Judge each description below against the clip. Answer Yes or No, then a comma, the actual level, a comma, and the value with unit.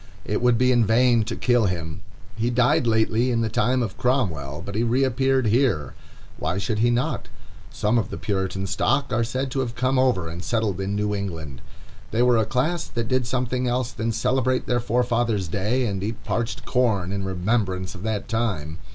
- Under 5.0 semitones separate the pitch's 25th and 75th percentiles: Yes, average, 4.1 semitones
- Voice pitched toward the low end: Yes, low, 115 Hz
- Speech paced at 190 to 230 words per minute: Yes, average, 195 wpm